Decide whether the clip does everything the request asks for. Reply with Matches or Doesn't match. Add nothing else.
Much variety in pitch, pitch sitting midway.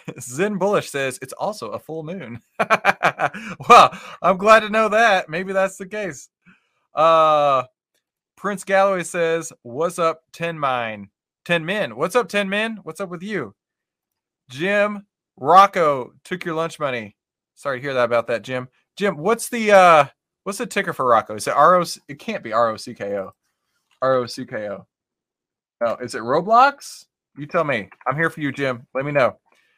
Matches